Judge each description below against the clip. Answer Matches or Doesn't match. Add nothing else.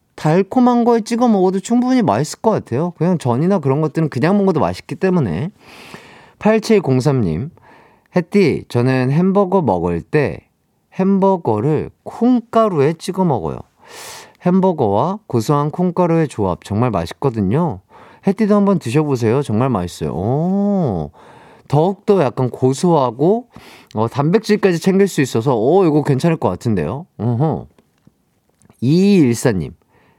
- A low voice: Doesn't match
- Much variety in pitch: Matches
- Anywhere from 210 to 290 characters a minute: Matches